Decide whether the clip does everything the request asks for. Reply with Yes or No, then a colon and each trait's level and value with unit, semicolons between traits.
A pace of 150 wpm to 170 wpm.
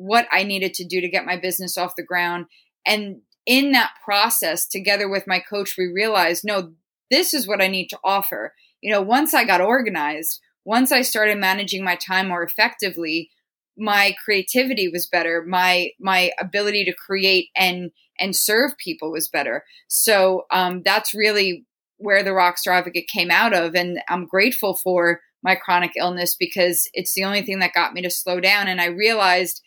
No: average, 185 wpm